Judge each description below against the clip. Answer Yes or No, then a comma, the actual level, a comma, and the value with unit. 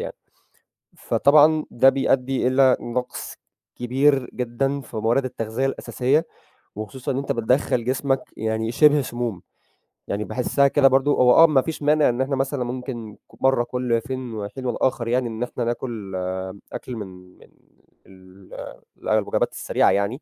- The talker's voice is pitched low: Yes, low, 125 Hz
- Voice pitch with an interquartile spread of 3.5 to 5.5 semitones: No, narrow, 2.6 semitones